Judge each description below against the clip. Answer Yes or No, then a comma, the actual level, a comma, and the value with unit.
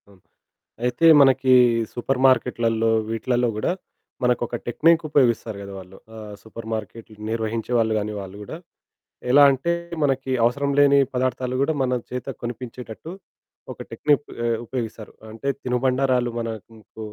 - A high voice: No, low, 120 Hz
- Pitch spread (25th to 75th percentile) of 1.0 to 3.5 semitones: Yes, average, 2.9 semitones